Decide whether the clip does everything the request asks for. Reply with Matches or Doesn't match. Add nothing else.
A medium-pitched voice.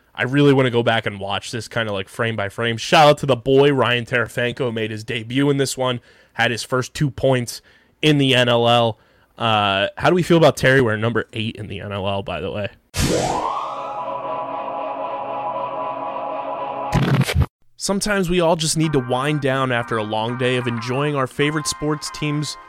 Doesn't match